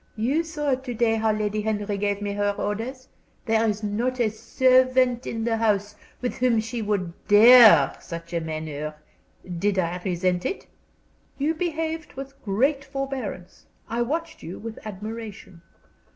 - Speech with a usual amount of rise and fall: Yes, average, 4.0 semitones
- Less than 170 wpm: Yes, average, 150 wpm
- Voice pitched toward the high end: Yes, high, 225 Hz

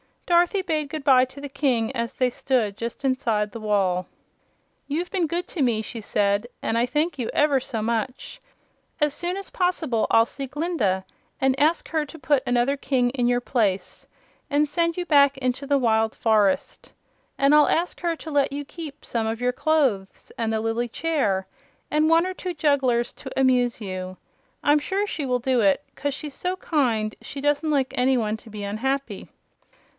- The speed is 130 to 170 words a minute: No, average, 190 wpm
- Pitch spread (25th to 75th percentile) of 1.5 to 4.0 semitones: No, average, 4.7 semitones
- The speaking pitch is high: Yes, very high, 265 Hz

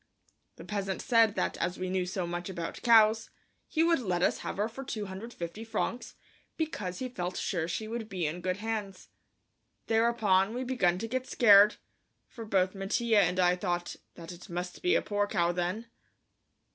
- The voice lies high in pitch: Yes, high, 200 Hz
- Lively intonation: No, average, 4.0 semitones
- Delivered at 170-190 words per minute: Yes, average, 180 wpm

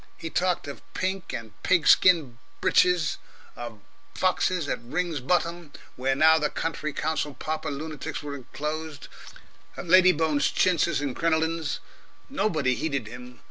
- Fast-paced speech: No, average, 140 wpm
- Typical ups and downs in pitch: Yes, average, 3.4 semitones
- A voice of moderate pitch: Yes, medium, 155 Hz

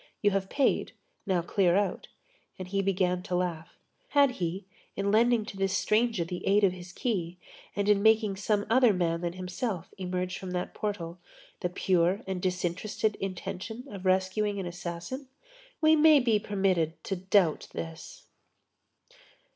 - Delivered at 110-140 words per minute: No, average, 155 wpm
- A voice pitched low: No, high, 190 Hz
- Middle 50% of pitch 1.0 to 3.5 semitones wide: Yes, average, 2.8 semitones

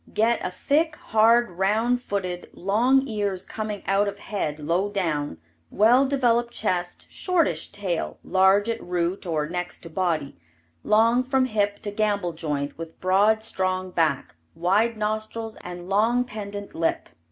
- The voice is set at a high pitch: Yes, high, 205 Hz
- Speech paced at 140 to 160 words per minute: Yes, average, 145 wpm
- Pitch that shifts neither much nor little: Yes, average, 4.0 semitones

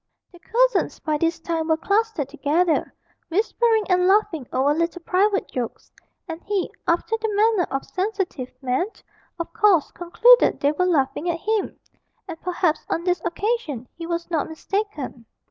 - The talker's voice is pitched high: Yes, very high, 345 Hz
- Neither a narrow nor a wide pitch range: Yes, average, 4.5 semitones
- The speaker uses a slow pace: No, average, 155 wpm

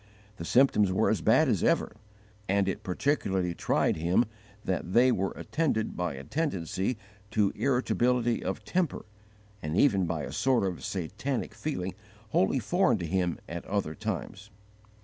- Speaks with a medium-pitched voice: No, low, 100 Hz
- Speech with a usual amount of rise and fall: No, wide, 5.7 semitones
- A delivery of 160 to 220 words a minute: No, average, 150 wpm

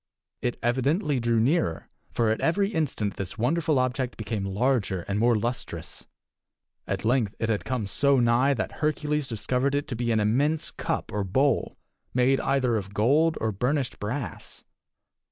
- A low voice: Yes, low, 125 Hz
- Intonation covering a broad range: No, average, 4.2 semitones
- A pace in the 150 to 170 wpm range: Yes, average, 160 wpm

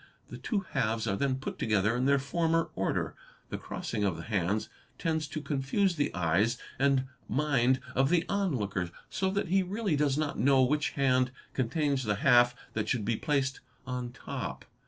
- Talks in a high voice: No, low, 135 Hz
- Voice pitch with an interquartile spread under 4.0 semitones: No, average, 4.7 semitones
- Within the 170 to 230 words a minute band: Yes, average, 175 wpm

